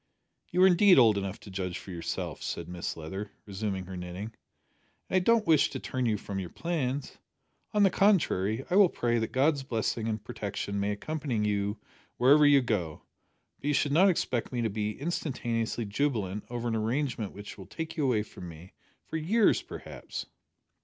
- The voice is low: Yes, low, 115 Hz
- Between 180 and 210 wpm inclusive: Yes, average, 185 wpm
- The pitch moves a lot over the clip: Yes, wide, 6.6 semitones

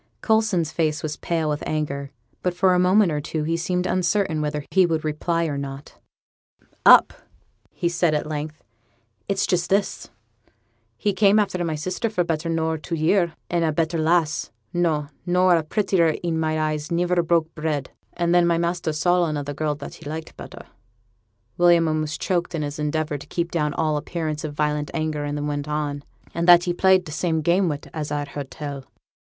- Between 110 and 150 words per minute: No, average, 195 wpm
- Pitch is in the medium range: Yes, medium, 160 Hz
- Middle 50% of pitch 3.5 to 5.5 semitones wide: No, narrow, 2.6 semitones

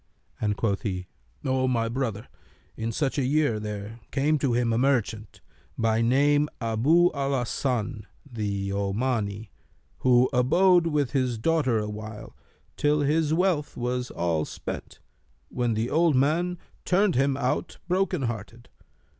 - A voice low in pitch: Yes, low, 125 Hz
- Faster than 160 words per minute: No, average, 140 wpm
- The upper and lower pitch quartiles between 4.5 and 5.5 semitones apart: Yes, average, 4.8 semitones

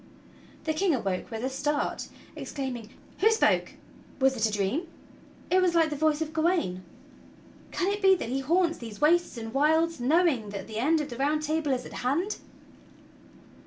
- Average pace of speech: Yes, average, 180 wpm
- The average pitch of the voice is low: No, very high, 295 Hz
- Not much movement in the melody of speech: No, wide, 5.4 semitones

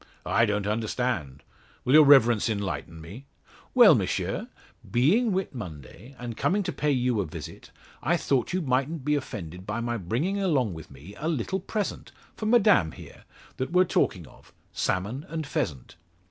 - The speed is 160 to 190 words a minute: Yes, average, 165 wpm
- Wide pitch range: Yes, wide, 7.7 semitones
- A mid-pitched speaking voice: No, low, 125 Hz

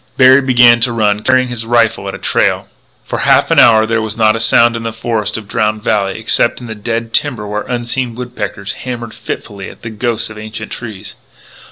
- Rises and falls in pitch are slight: Yes, narrow, 1.9 semitones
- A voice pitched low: Yes, low, 115 Hz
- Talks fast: Yes, fast, 210 wpm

